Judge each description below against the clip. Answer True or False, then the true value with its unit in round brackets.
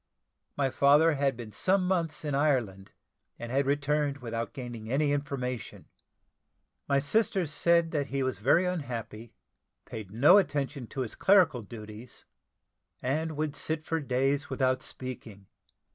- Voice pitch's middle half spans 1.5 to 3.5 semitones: False (4.0 semitones)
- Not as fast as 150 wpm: True (140 wpm)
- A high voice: False (140 Hz)